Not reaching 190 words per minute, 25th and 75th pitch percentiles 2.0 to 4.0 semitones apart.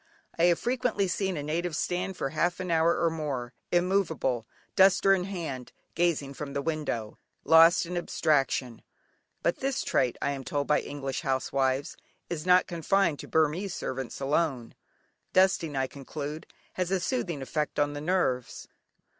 No: average, 155 wpm; average, 4.5 semitones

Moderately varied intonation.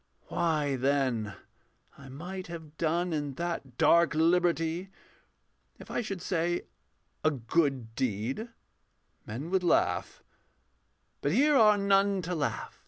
Yes: average, 4.6 semitones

